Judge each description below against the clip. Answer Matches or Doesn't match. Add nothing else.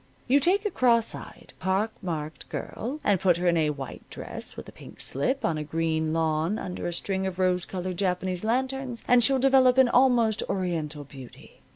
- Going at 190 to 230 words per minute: Matches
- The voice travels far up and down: Matches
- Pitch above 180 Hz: Matches